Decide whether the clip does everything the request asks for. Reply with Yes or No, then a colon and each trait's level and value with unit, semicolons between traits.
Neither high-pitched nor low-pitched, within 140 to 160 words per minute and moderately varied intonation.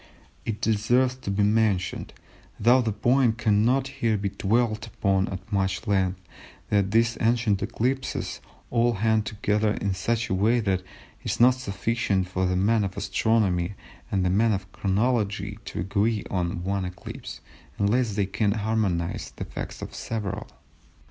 No: low, 105 Hz; average, 155 wpm; average, 3.0 semitones